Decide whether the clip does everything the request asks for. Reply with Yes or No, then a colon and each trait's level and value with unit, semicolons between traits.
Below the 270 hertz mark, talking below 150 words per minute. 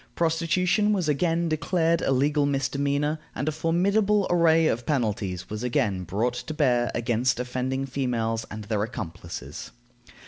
Yes: low, 135 Hz; average, 140 wpm